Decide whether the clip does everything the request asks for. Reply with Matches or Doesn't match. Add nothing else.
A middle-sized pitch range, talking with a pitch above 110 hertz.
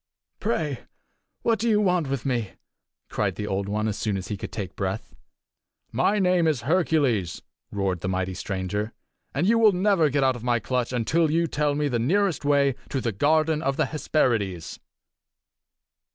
Doesn't match